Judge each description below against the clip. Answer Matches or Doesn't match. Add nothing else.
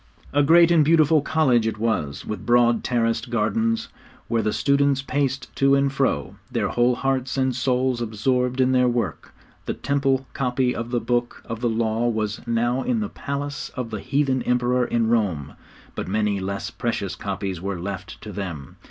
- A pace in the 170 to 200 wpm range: Matches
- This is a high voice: Doesn't match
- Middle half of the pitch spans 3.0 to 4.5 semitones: Matches